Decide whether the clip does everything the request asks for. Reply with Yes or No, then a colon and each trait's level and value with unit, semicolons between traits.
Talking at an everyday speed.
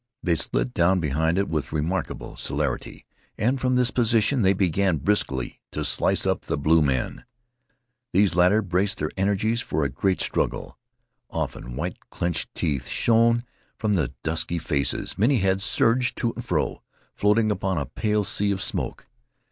Yes: average, 160 wpm